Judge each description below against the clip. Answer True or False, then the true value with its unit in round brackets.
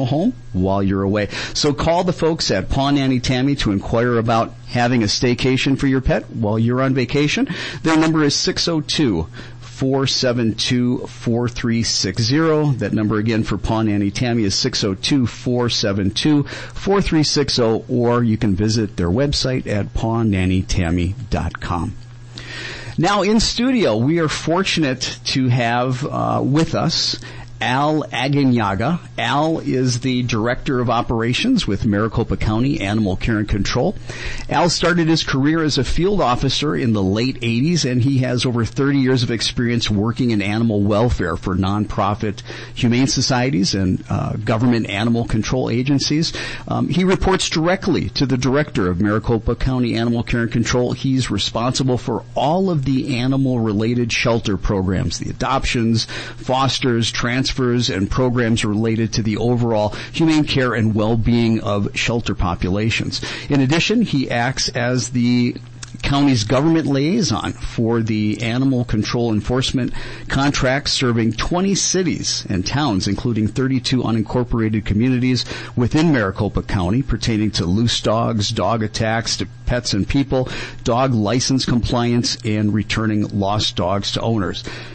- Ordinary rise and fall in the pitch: True (3.5 semitones)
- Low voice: True (120 Hz)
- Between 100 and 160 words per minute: True (140 wpm)